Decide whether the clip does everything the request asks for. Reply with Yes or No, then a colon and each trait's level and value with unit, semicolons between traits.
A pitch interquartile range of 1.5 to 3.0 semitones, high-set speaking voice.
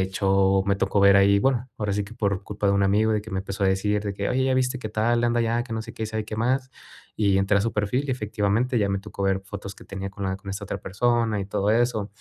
No: narrow, 2.6 semitones; low, 105 Hz